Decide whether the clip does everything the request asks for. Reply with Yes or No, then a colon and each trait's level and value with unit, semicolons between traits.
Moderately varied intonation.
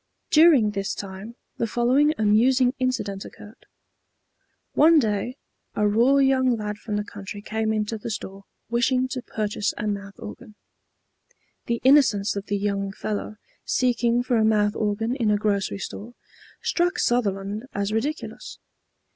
Yes: average, 3.4 semitones